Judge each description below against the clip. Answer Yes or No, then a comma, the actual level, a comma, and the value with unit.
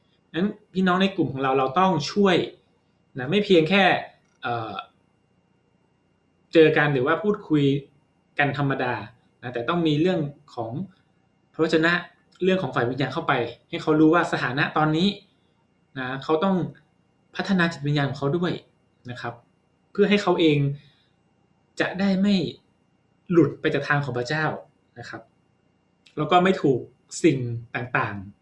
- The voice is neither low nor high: Yes, medium, 155 Hz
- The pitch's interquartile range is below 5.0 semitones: Yes, average, 4.3 semitones